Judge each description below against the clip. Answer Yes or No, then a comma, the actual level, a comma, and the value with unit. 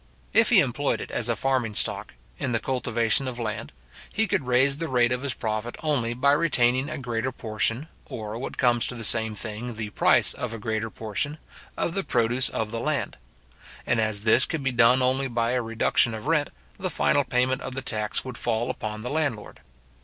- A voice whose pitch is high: No, low, 125 Hz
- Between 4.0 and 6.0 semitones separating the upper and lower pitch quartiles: No, average, 3.0 semitones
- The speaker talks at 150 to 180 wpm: No, fast, 205 wpm